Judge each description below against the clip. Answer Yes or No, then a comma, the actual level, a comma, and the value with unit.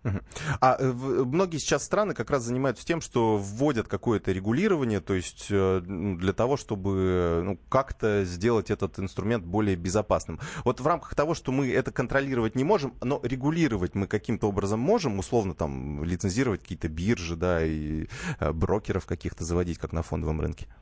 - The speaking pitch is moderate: No, low, 105 Hz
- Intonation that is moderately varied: No, wide, 6.0 semitones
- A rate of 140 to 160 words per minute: Yes, average, 155 wpm